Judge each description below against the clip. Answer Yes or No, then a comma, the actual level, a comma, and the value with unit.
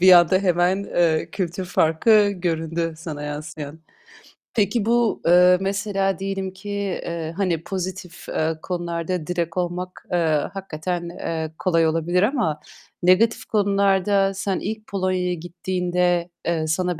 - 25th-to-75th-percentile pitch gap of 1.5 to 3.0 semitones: Yes, average, 2.7 semitones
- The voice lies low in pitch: No, medium, 180 Hz